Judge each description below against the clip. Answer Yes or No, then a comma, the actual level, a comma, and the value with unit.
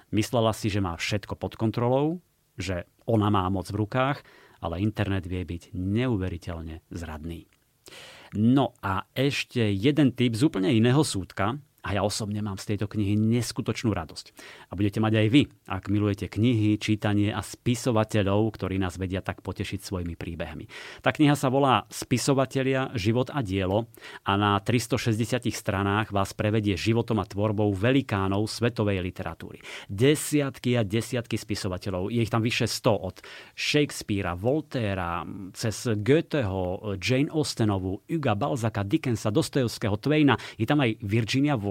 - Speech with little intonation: No, average, 4.2 semitones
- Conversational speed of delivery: Yes, average, 145 wpm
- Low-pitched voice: Yes, low, 110 Hz